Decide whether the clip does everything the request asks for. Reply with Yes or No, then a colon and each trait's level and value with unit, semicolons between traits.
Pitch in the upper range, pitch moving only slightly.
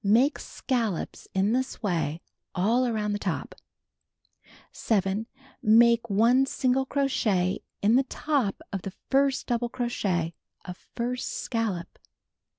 No: high, 225 Hz; average, 4.3 semitones